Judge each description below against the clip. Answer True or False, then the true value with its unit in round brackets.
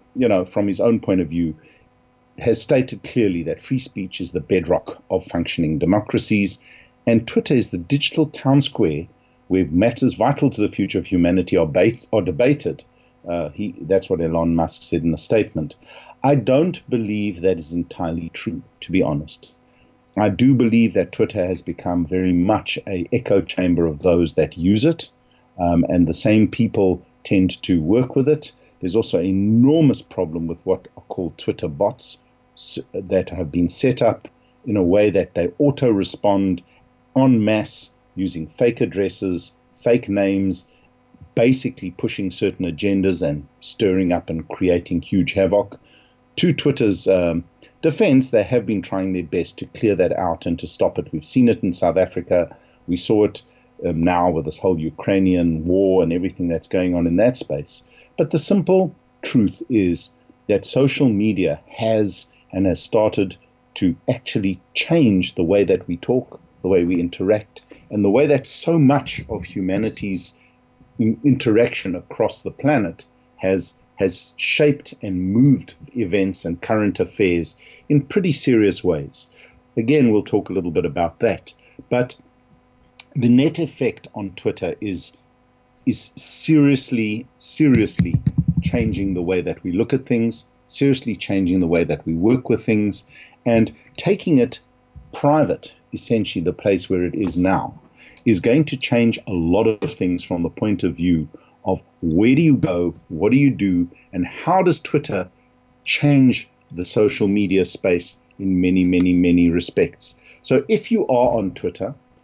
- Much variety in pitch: True (6.0 semitones)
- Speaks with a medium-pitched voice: False (100 Hz)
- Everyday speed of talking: True (165 wpm)